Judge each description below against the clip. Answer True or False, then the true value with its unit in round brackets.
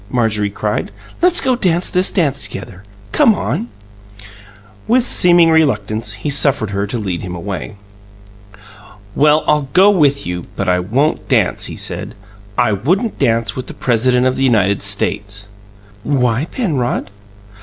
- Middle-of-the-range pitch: False (125 Hz)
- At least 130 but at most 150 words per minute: True (145 wpm)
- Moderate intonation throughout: False (7.2 semitones)